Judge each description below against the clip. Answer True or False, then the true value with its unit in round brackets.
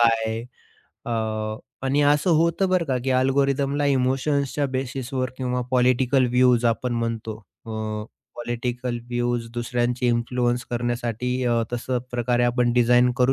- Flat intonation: True (1.7 semitones)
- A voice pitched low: True (125 Hz)